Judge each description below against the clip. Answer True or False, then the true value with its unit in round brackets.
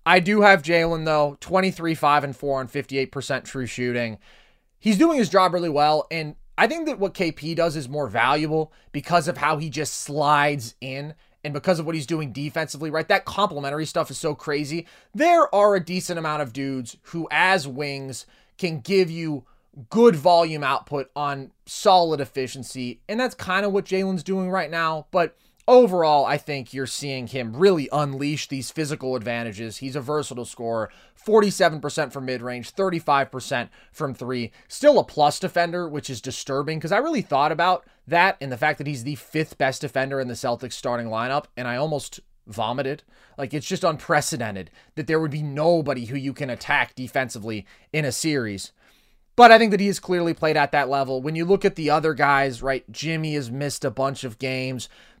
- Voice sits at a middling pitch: True (150 Hz)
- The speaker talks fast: False (190 wpm)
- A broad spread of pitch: False (4.1 semitones)